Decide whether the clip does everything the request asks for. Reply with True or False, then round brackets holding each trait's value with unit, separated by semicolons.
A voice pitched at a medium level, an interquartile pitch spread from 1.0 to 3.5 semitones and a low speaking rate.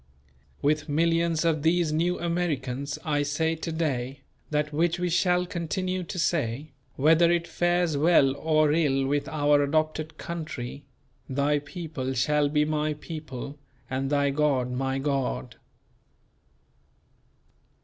True (150 Hz; 2.9 semitones; 130 wpm)